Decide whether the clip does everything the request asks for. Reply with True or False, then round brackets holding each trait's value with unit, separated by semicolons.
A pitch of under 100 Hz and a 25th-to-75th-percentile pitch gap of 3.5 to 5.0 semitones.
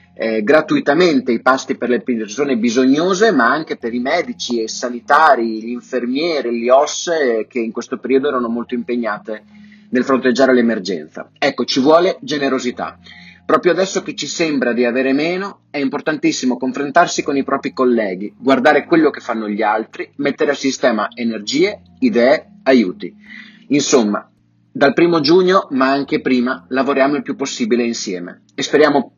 False (130 Hz; 3.8 semitones)